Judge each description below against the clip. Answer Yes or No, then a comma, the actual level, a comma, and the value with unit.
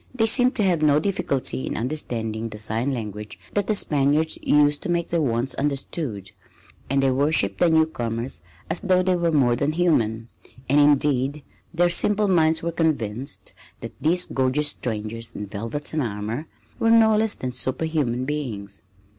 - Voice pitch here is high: No, medium, 145 Hz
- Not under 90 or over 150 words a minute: No, average, 165 wpm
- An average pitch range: No, wide, 5.9 semitones